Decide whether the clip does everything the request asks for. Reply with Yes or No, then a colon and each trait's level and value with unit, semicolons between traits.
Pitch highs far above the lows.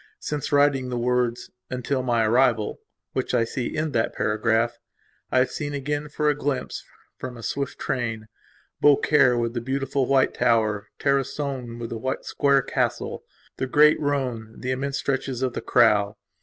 No: average, 3.0 semitones